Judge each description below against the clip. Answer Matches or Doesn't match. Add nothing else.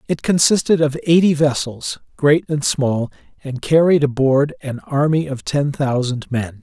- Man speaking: Matches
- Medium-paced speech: Matches